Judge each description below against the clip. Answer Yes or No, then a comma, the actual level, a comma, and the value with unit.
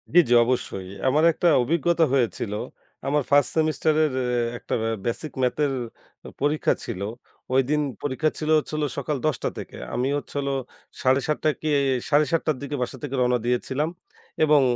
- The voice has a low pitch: No, medium, 145 Hz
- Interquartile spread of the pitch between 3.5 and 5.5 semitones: No, average, 3.1 semitones